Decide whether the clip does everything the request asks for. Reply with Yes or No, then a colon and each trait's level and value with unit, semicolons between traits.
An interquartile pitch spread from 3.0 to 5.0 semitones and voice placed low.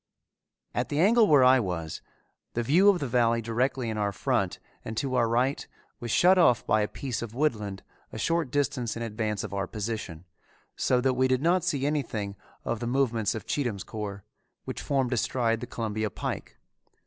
Yes: average, 4.0 semitones; low, 120 Hz